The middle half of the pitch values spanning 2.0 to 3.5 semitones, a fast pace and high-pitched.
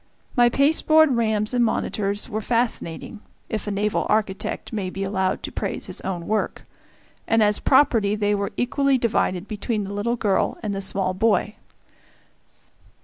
No: average, 2.9 semitones; average, 155 wpm; high, 210 Hz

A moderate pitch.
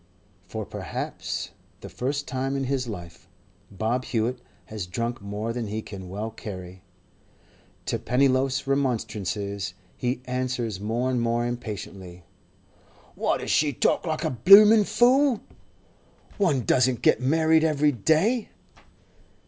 No: low, 125 Hz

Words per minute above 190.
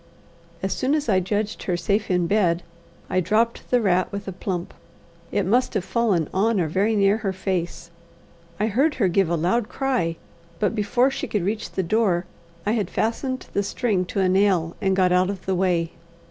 Yes: average, 200 wpm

